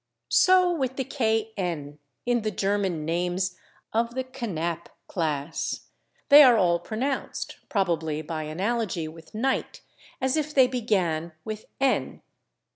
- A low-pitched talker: No, high, 205 Hz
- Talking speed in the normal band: No, slow, 125 wpm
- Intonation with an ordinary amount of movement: No, wide, 7.0 semitones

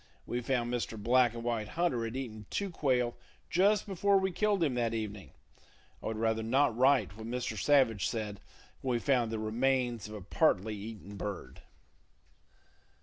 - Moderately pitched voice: No, low, 120 Hz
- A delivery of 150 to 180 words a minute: Yes, average, 170 wpm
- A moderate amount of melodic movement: Yes, average, 3.6 semitones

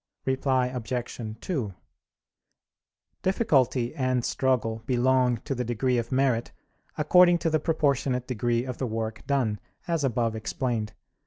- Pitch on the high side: No, low, 125 Hz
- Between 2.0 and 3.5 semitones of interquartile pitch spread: Yes, narrow, 2.5 semitones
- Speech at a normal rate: No, slow, 130 wpm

